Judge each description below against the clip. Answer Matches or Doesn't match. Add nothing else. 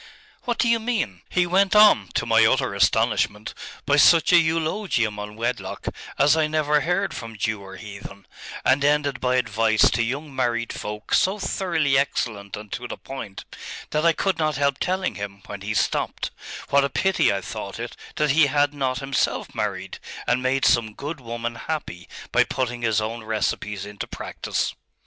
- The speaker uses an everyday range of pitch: Doesn't match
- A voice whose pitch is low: Matches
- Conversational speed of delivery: Matches